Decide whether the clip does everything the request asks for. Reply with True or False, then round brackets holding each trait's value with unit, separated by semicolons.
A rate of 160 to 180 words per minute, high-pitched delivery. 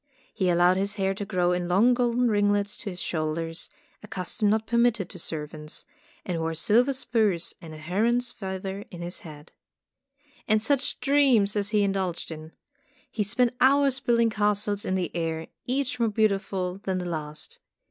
True (170 wpm; 200 Hz)